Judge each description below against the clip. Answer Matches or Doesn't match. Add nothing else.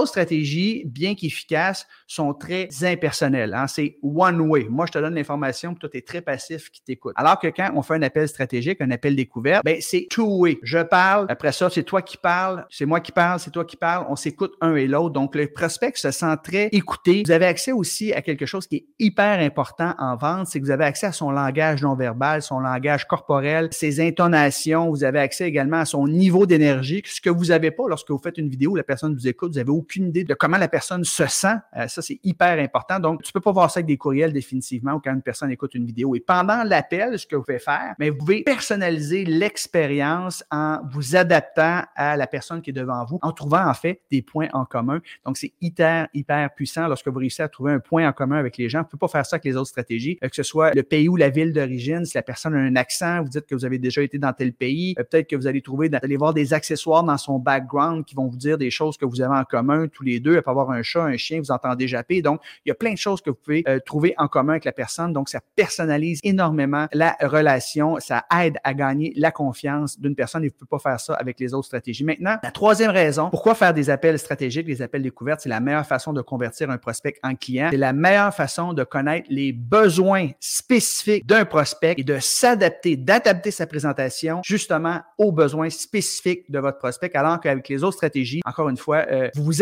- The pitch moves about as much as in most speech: Matches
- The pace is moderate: Doesn't match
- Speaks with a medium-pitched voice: Matches